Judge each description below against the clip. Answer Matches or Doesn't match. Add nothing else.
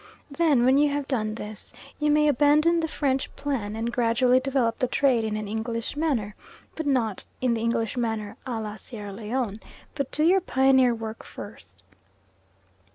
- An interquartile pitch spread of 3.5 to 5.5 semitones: Matches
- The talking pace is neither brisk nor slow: Matches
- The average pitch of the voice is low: Doesn't match